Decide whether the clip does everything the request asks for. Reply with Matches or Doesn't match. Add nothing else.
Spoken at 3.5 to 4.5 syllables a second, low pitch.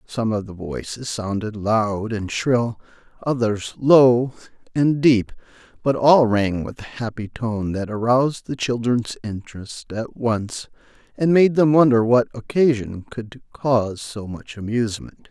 Matches